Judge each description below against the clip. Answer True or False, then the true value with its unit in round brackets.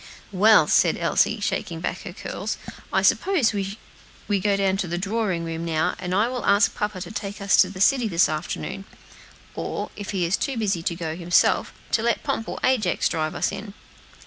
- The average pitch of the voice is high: True (195 Hz)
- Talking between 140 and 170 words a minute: False (195 wpm)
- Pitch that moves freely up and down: False (3.4 semitones)